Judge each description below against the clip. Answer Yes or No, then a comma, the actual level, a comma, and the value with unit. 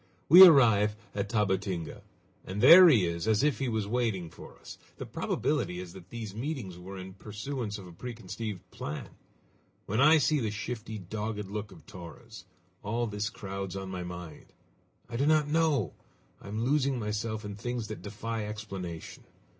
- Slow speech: No, average, 170 wpm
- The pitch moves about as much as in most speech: Yes, average, 3.9 semitones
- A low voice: Yes, low, 105 Hz